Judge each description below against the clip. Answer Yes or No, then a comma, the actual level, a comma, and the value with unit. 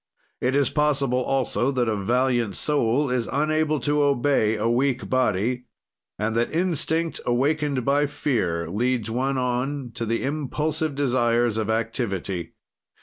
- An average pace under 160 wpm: Yes, average, 140 wpm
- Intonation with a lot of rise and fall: No, average, 3.7 semitones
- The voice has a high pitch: No, low, 125 Hz